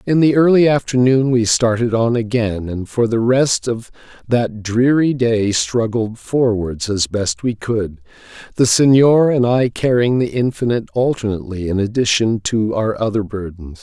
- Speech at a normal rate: Yes, average, 155 wpm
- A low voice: Yes, low, 115 Hz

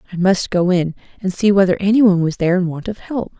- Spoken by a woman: Yes, female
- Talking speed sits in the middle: No, fast, 250 wpm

